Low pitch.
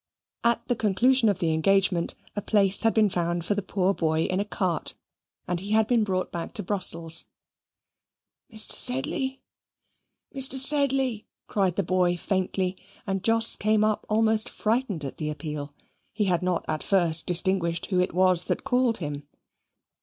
No: high, 195 Hz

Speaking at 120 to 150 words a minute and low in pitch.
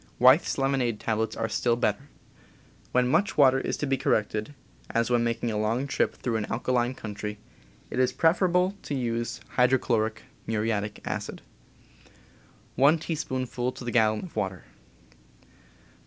Yes: average, 140 wpm; low, 120 Hz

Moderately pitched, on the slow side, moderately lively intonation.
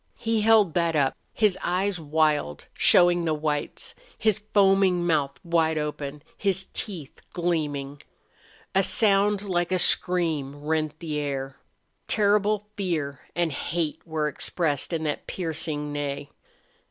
Yes: medium, 165 Hz; slow, 130 wpm; average, 4.3 semitones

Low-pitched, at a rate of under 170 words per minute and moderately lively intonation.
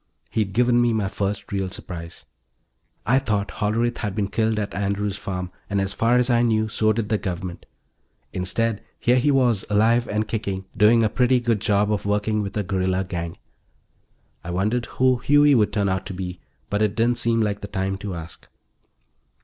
No: low, 105 Hz; average, 190 wpm; average, 3.0 semitones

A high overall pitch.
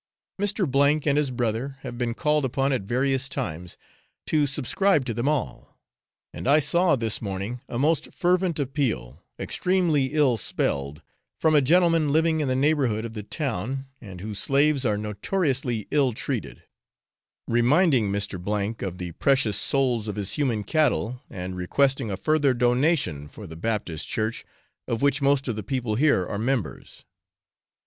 No: low, 130 Hz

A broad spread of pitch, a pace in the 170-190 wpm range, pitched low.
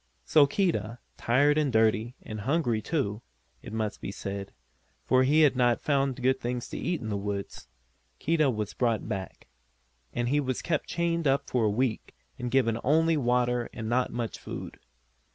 No: average, 4.4 semitones; average, 175 wpm; low, 125 Hz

